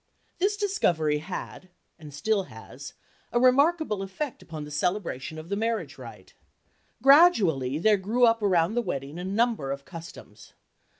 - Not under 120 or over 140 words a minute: Yes, slow, 135 wpm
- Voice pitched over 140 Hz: Yes, medium, 185 Hz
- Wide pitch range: Yes, wide, 7.6 semitones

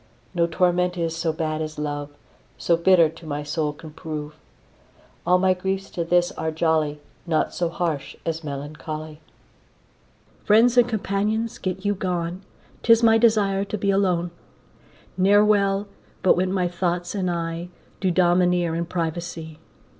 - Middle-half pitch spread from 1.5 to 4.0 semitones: Yes, average, 3.1 semitones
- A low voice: No, medium, 175 Hz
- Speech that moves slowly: No, average, 150 wpm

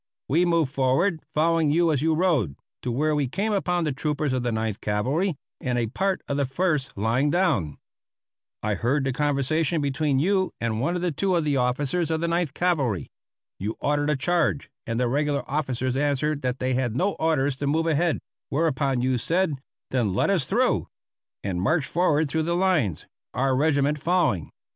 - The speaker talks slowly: No, average, 185 wpm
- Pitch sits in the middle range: Yes, medium, 145 Hz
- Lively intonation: No, average, 4.4 semitones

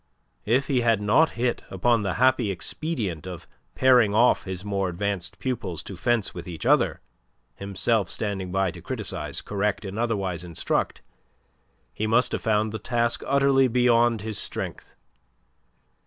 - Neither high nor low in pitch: No, low, 105 Hz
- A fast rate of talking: No, average, 150 wpm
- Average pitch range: Yes, average, 3.9 semitones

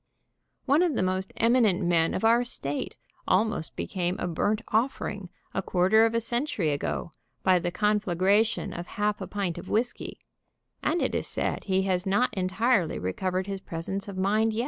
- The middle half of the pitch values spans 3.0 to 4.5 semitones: Yes, average, 3.7 semitones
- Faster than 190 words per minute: No, average, 180 wpm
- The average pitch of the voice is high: Yes, high, 195 Hz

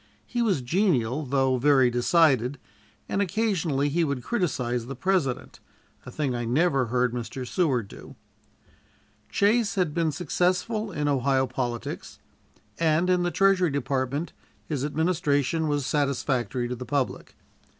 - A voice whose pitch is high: No, medium, 145 Hz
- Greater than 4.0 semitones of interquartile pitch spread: Yes, wide, 5.6 semitones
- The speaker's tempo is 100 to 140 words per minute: Yes, slow, 135 wpm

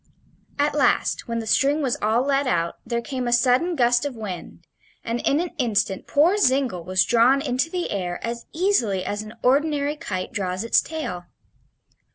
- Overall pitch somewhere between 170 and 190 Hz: No, high, 245 Hz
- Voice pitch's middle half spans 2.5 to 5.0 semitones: No, wide, 5.4 semitones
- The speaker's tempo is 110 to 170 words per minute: No, average, 180 wpm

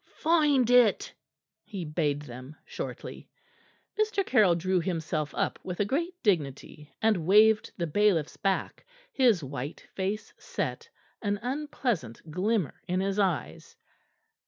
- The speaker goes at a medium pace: No, slow, 125 wpm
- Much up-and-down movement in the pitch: Yes, wide, 5.9 semitones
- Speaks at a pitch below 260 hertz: Yes, high, 190 Hz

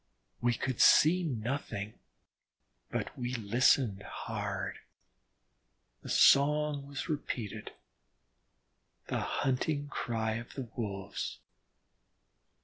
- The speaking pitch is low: Yes, low, 125 Hz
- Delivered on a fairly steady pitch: No, average, 4.3 semitones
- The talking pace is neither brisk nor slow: No, slow, 85 wpm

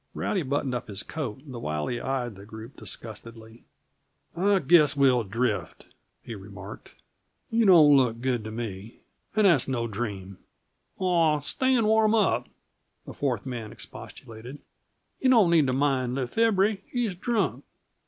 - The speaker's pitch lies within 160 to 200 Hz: No, low, 130 Hz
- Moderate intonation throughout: No, wide, 7.5 semitones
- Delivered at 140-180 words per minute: Yes, average, 155 wpm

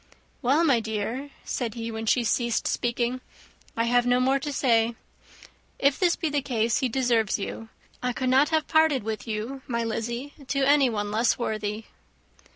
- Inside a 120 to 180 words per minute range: Yes, average, 170 wpm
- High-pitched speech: Yes, high, 245 Hz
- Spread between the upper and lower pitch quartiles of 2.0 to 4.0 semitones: Yes, average, 3.2 semitones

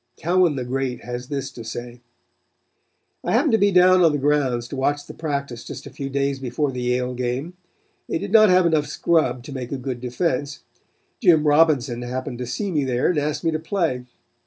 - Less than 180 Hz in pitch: Yes, medium, 140 Hz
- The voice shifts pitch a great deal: No, average, 4.5 semitones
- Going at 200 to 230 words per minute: Yes, fast, 205 wpm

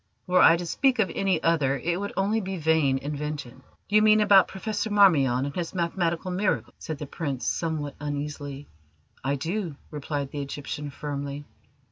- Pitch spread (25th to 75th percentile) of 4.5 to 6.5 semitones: Yes, average, 4.9 semitones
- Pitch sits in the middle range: Yes, medium, 160 Hz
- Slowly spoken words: No, average, 165 wpm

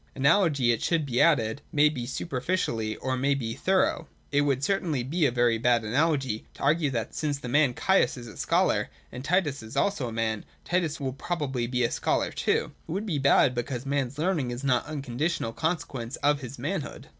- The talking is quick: Yes, fast, 215 wpm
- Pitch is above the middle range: No, medium, 140 Hz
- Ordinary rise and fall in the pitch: Yes, average, 4.2 semitones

